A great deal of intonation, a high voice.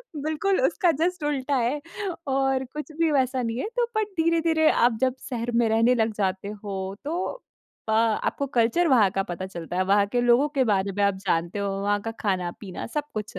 Yes: wide, 6.4 semitones; high, 240 Hz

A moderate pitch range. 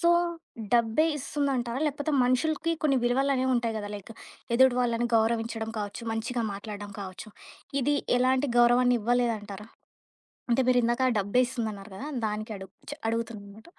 Yes: average, 3.0 semitones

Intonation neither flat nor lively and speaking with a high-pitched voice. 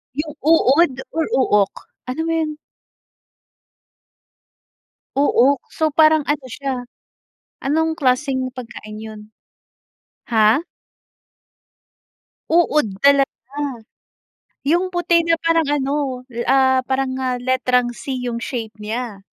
Yes: average, 3.8 semitones; very high, 270 Hz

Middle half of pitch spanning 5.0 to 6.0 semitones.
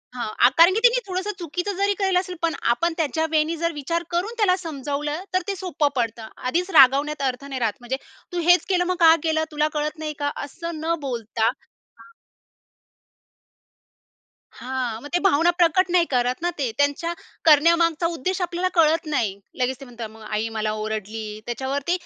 Yes: wide, 5.5 semitones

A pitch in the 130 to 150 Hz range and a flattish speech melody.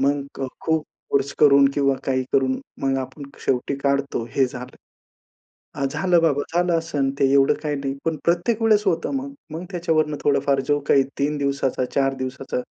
No: medium, 140 Hz; average, 3.1 semitones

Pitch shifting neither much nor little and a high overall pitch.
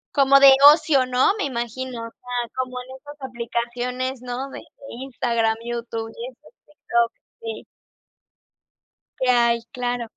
No: narrow, 1.7 semitones; high, 245 Hz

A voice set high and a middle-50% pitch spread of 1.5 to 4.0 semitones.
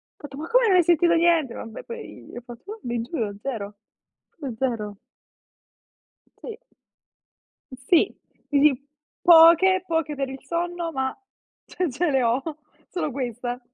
No: very high, 285 Hz; wide, 5.8 semitones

